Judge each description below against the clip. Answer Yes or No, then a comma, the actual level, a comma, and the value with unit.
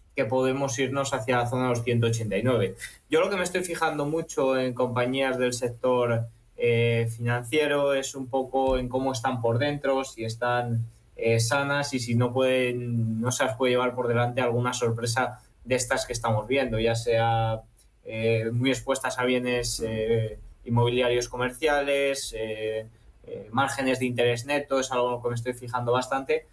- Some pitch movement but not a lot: No, narrow, 2.2 semitones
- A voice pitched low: Yes, low, 125 Hz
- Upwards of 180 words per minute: No, average, 170 wpm